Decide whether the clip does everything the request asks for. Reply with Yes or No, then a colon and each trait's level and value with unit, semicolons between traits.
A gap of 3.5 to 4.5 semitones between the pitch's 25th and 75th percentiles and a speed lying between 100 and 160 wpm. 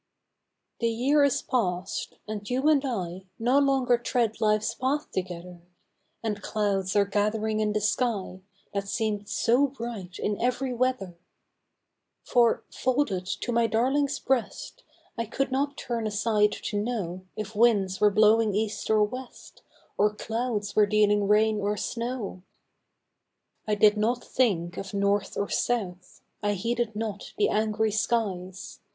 No: average, 3.0 semitones; average, 145 wpm